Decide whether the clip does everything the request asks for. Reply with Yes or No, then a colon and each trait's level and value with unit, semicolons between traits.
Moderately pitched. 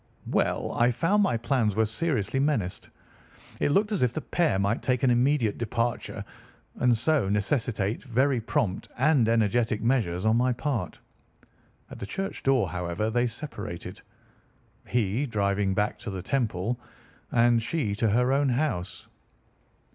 No: low, 120 Hz